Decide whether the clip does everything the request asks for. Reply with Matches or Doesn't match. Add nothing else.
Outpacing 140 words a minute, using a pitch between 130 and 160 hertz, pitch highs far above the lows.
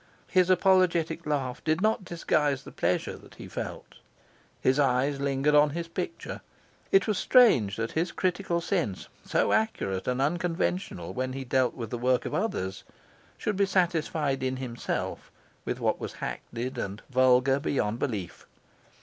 Matches